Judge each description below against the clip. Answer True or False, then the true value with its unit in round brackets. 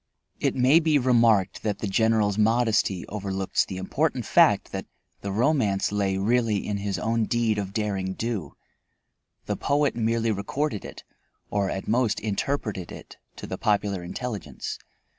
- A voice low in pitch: True (105 Hz)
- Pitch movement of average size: True (3.2 semitones)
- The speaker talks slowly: False (150 wpm)